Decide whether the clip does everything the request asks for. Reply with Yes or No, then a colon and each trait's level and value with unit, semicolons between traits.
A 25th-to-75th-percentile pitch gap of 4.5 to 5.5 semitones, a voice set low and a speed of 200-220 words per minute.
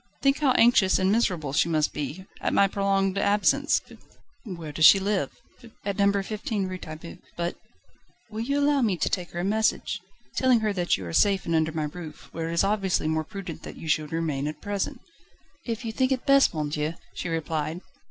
No: average, 4.9 semitones; medium, 185 Hz; fast, 205 wpm